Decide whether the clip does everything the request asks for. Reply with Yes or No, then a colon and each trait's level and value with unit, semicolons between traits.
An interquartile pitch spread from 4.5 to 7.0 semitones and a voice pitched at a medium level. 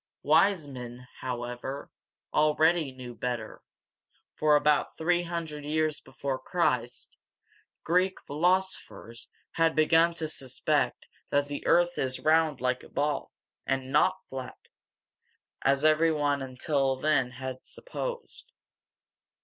No: average, 3.9 semitones; medium, 145 Hz